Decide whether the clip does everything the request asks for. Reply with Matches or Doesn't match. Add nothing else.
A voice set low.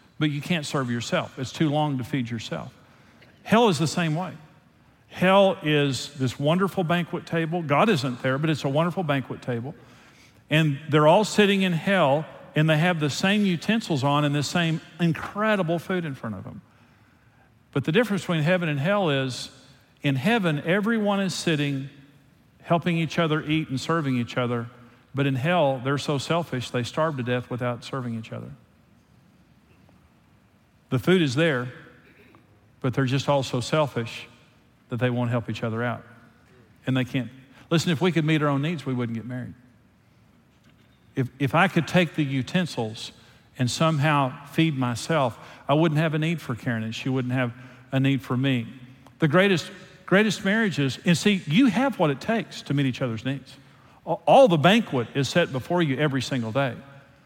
Doesn't match